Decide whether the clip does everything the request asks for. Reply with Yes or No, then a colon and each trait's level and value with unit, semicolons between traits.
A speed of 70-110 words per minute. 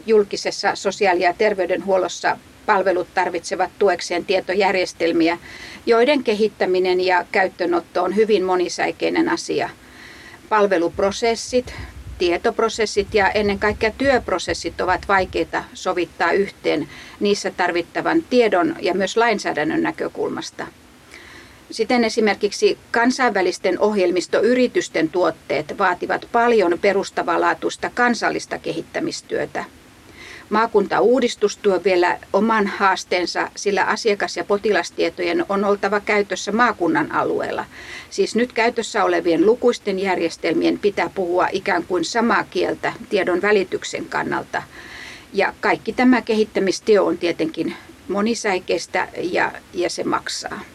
Yes: average, 100 wpm